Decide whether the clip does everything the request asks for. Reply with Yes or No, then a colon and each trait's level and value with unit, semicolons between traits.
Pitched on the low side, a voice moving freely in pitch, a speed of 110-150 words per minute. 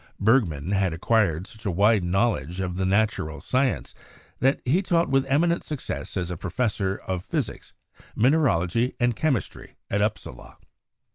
Yes: low, 105 Hz; wide, 6.0 semitones; average, 145 wpm